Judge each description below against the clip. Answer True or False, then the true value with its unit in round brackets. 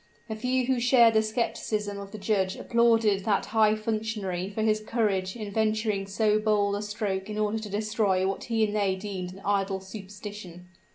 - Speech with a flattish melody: True (1.9 semitones)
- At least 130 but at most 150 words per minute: False (185 wpm)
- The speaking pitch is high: True (210 Hz)